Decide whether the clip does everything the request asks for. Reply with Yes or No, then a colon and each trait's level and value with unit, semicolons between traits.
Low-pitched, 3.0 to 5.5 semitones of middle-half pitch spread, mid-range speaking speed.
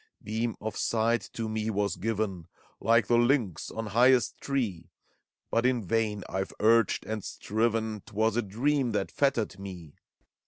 No: low, 110 Hz; narrow, 2.5 semitones; average, 155 wpm